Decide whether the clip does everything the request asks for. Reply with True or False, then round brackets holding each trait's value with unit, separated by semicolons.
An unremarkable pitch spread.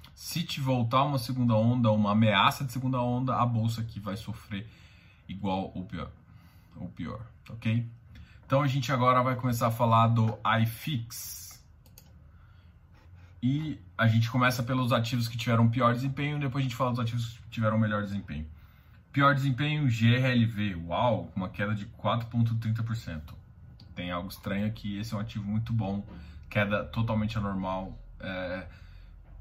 True (4.2 semitones)